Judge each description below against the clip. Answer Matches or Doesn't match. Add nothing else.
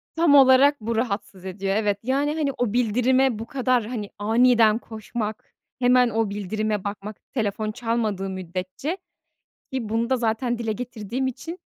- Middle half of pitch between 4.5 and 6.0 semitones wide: Doesn't match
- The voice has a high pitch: Matches